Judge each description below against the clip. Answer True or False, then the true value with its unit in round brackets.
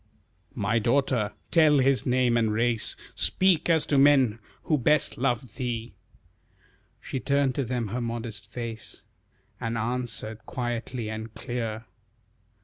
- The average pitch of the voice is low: True (120 Hz)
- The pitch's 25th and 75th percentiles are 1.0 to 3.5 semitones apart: True (3.0 semitones)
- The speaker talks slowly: True (130 wpm)